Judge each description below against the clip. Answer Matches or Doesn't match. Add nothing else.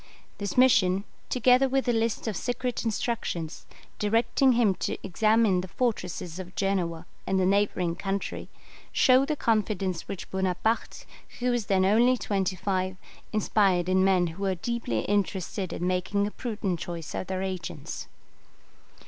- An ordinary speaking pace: Matches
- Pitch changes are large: Doesn't match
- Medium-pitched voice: Doesn't match